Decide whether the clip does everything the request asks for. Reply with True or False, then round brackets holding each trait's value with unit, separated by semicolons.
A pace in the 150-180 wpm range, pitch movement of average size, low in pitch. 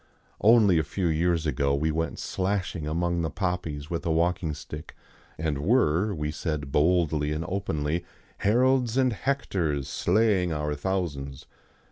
False (140 wpm; 4.1 semitones; 85 Hz)